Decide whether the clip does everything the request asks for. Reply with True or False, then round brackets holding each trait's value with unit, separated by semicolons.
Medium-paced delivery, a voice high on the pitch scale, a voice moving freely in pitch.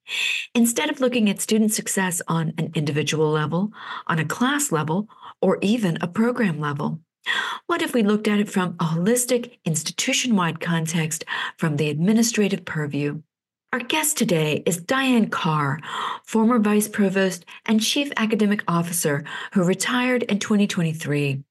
True (145 wpm; 195 Hz; 6.2 semitones)